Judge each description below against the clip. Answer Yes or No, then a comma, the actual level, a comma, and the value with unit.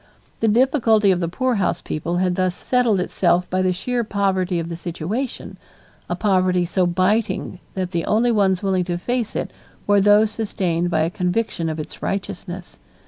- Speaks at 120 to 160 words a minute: No, average, 175 wpm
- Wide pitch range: No, average, 3.3 semitones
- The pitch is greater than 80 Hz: Yes, medium, 185 Hz